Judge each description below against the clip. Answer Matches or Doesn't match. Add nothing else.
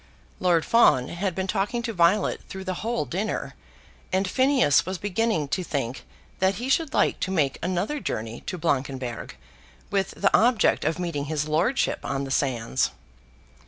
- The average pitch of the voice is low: Doesn't match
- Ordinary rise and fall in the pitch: Doesn't match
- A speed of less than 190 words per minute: Matches